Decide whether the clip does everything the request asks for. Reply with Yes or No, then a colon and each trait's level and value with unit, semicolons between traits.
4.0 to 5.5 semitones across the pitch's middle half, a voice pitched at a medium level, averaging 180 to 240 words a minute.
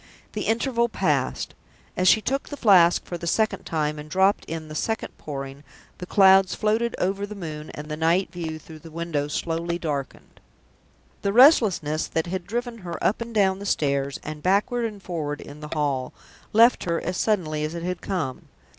Yes: average, 5.0 semitones; medium, 175 Hz; average, 190 wpm